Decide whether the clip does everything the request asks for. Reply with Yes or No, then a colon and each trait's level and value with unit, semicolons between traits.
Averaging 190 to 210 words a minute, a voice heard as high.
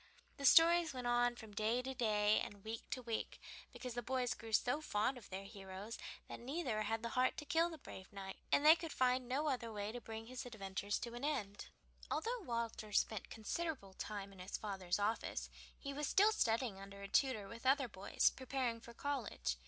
Yes: fast, 205 wpm; high, 235 Hz